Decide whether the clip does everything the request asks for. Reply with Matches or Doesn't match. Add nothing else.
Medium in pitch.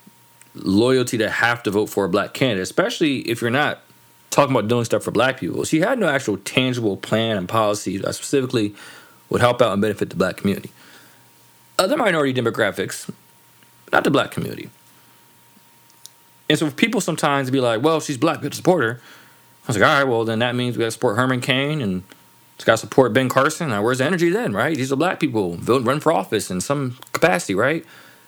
Doesn't match